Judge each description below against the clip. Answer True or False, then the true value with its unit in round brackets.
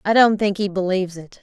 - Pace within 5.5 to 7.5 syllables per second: True (6.0 syllables/s)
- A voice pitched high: True (195 Hz)